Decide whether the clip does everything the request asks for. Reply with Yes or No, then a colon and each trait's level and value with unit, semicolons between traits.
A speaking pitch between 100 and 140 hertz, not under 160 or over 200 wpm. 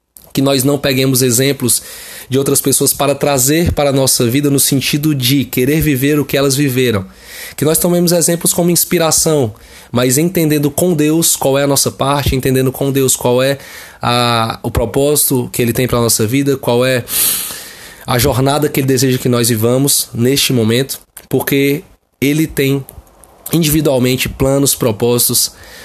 Yes: low, 135 Hz; average, 165 wpm